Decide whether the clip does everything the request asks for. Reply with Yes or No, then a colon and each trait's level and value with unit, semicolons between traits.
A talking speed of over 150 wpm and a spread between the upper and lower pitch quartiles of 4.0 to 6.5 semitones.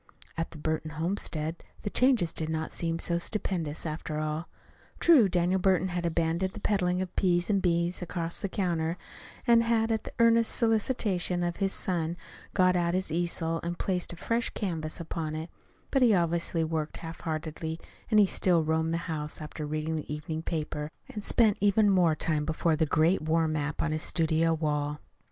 No: average, 185 wpm; average, 2.9 semitones